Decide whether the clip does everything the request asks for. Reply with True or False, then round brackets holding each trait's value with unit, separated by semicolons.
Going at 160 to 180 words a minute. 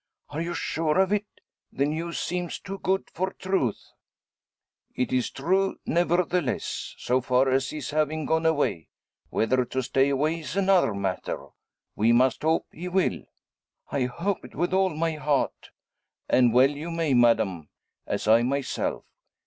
False (150 wpm)